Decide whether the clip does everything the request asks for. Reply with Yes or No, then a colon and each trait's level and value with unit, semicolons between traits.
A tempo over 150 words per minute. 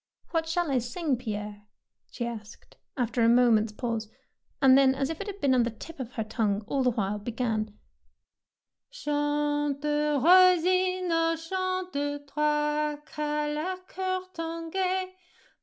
No: average, 145 wpm